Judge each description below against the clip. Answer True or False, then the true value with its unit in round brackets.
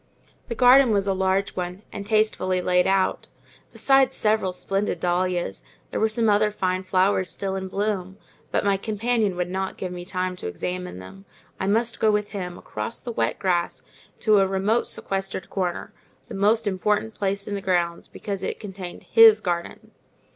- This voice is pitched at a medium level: False (195 Hz)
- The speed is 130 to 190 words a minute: True (175 wpm)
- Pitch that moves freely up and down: False (2.6 semitones)